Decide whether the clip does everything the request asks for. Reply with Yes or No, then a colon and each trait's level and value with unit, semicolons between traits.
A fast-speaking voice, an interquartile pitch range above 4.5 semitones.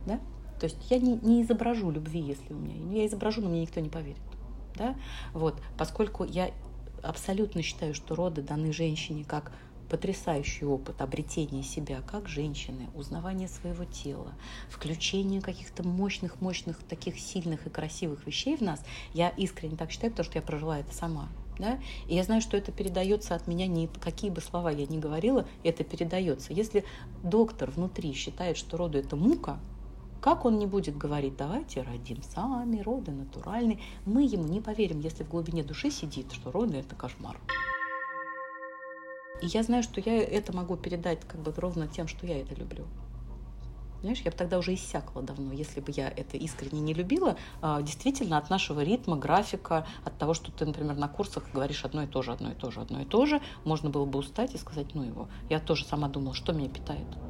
Yes: fast, 185 wpm; average, 5.2 semitones